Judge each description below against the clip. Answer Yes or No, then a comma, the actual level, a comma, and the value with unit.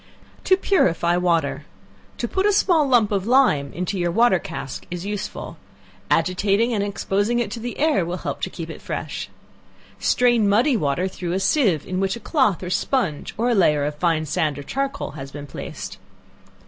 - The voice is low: No, high, 195 Hz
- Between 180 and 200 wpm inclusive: Yes, average, 185 wpm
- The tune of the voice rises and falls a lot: Yes, wide, 6.0 semitones